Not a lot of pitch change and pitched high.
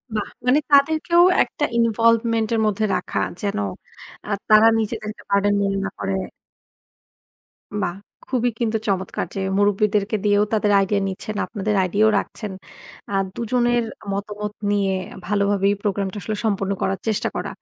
Yes: narrow, 2.1 semitones; high, 210 Hz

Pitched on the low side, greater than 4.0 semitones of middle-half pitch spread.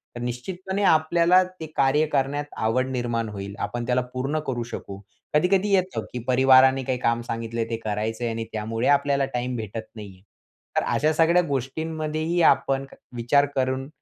Yes: low, 130 Hz; average, 4.8 semitones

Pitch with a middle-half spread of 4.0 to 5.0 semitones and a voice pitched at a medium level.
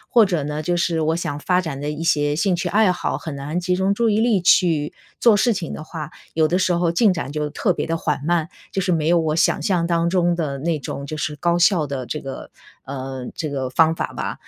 No: average, 3.2 semitones; medium, 165 Hz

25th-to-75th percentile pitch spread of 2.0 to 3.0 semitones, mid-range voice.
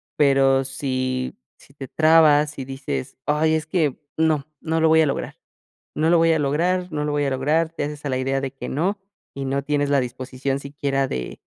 Yes: average, 2.7 semitones; medium, 145 Hz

